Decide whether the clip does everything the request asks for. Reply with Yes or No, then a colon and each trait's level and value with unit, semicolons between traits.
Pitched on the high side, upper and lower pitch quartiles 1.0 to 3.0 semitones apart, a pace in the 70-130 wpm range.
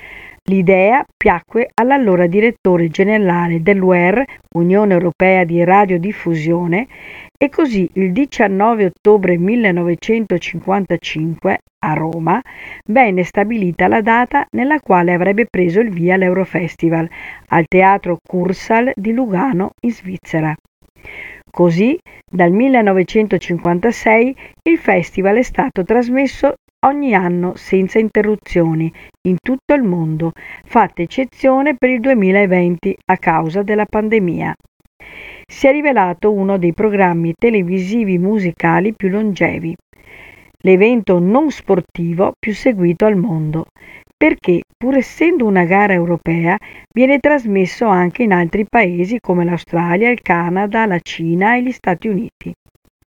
No: high, 195 Hz; average, 4.4 semitones; slow, 115 wpm